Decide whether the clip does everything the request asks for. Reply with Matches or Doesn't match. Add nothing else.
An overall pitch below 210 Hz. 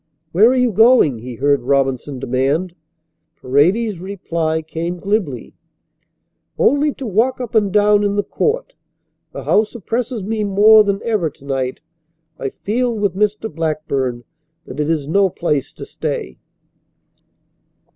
Matches